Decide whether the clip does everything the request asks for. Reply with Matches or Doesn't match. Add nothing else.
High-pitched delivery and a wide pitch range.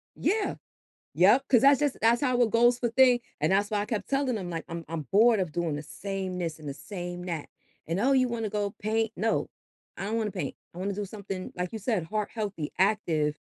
Doesn't match